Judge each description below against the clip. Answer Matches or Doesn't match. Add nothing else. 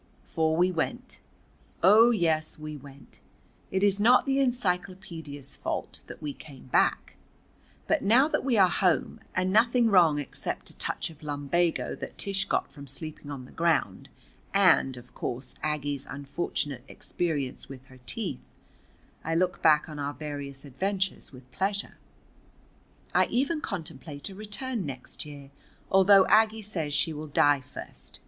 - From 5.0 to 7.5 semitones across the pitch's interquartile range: Matches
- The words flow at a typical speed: Matches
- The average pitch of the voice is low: Doesn't match